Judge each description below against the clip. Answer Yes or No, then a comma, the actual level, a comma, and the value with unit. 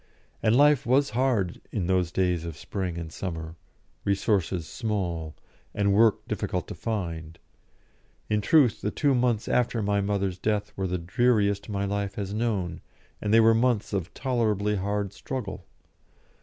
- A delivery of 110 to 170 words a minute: Yes, average, 155 wpm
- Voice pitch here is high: No, low, 100 Hz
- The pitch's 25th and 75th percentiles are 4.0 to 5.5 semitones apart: No, average, 3.5 semitones